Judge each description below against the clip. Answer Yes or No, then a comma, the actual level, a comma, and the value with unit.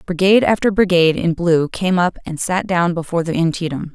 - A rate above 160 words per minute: Yes, average, 200 wpm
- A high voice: No, medium, 175 Hz